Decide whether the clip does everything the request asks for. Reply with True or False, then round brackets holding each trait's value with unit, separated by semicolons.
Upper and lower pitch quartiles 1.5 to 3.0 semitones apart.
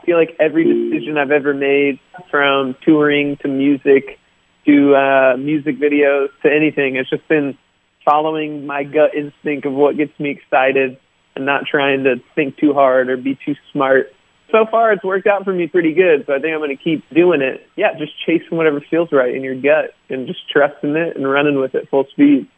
True (2.7 semitones)